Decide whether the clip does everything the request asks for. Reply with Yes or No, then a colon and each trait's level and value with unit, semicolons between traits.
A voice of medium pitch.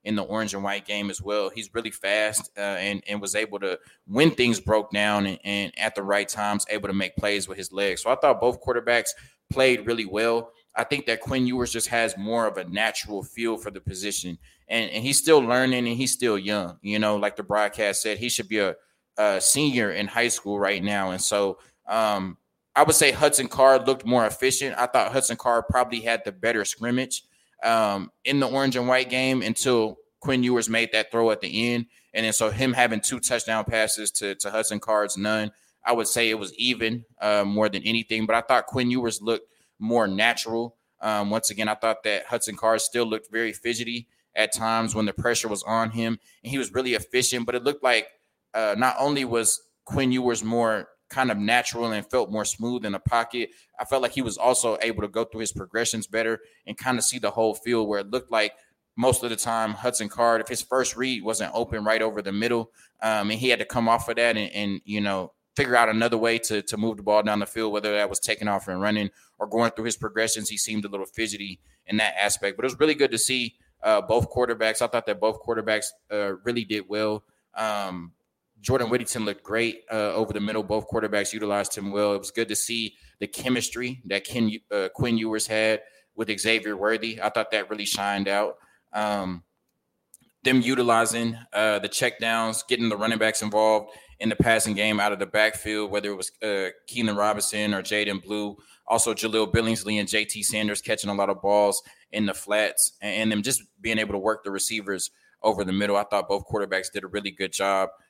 No: low, 110 Hz